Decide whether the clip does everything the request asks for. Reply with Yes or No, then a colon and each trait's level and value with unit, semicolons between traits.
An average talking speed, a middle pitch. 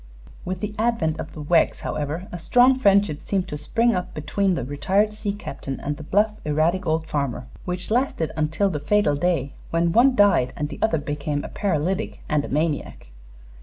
Yes: average, 190 wpm; medium, 170 Hz